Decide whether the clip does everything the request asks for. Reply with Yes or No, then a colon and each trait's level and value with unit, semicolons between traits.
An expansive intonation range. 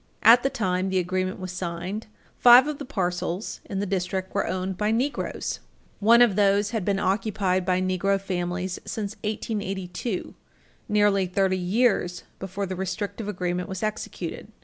No: narrow, 2.4 semitones